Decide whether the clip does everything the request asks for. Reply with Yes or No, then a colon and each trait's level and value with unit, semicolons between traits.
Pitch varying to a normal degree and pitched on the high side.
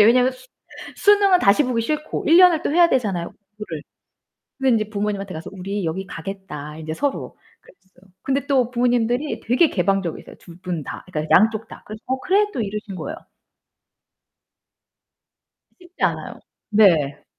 No: wide, 6.2 semitones; high, 215 Hz